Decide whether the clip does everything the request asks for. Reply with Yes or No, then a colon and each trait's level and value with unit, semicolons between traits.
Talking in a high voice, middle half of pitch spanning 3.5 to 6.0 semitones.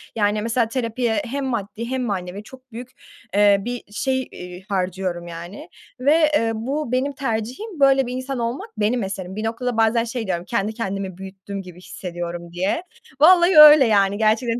Yes: high, 225 Hz; average, 4.9 semitones